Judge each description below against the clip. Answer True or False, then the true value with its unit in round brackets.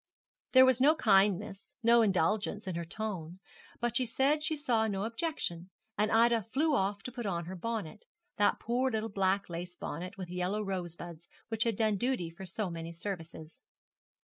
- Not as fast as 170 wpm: False (175 wpm)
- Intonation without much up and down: False (4.6 semitones)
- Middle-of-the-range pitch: False (205 Hz)